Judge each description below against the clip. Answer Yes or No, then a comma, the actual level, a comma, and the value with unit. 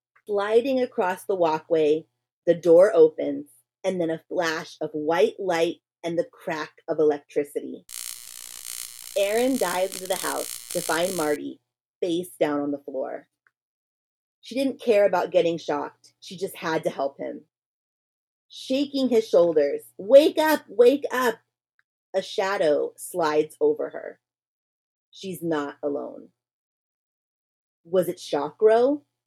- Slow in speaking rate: Yes, slow, 125 wpm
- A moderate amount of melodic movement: No, wide, 6.7 semitones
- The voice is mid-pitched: Yes, medium, 170 Hz